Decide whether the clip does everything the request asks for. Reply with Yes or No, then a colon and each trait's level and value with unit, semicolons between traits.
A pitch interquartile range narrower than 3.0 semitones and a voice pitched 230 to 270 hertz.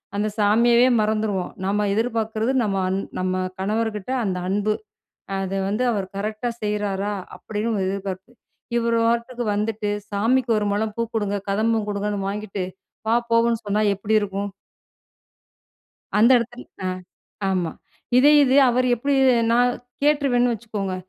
No: narrow, 2.6 semitones; high, 215 Hz